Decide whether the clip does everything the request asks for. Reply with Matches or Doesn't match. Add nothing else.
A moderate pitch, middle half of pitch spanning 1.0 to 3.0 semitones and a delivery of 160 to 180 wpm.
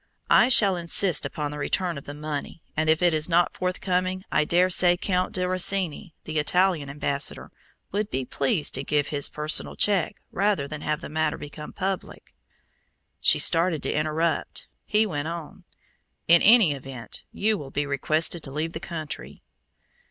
Doesn't match